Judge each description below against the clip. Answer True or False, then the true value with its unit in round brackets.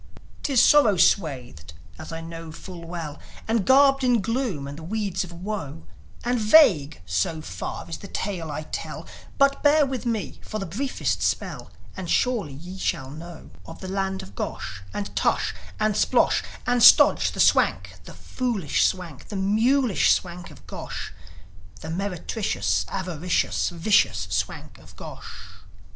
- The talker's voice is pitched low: False (190 Hz)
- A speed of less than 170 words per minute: True (155 wpm)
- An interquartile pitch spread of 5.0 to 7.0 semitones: True (5.6 semitones)